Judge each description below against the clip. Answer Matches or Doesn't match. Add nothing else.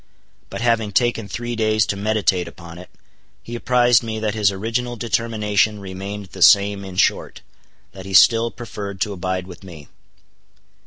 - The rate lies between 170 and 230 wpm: Doesn't match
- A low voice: Matches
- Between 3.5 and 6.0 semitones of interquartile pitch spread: Doesn't match